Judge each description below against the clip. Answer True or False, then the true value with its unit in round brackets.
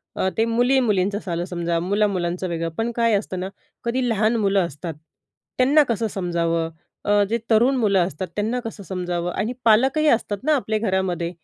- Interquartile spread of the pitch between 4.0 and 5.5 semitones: True (4.6 semitones)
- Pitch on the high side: True (205 Hz)